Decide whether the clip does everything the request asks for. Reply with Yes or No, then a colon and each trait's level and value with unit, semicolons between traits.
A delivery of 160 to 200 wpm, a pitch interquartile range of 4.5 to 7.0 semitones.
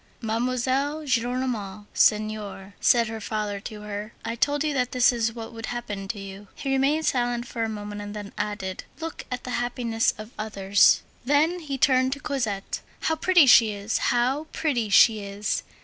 No: average, 180 wpm; average, 3.8 semitones